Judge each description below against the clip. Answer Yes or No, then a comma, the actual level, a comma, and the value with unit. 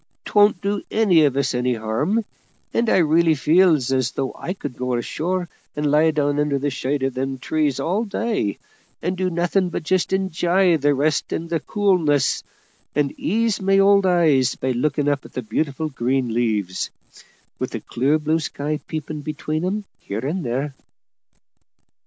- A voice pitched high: No, medium, 155 Hz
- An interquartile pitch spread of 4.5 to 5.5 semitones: Yes, average, 5.2 semitones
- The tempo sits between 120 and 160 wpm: No, average, 170 wpm